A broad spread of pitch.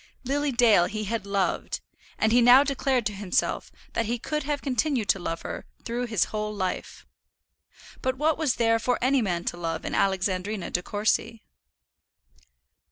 No: average, 4.4 semitones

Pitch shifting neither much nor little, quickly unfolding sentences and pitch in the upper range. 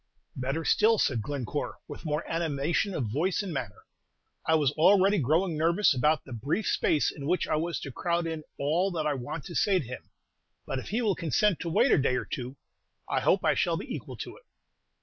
No: average, 4.3 semitones; fast, 215 wpm; medium, 160 Hz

